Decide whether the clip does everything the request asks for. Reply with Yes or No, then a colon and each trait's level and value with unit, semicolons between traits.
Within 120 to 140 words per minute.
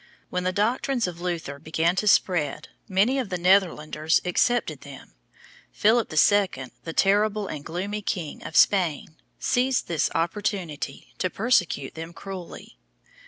Yes: slow, 135 wpm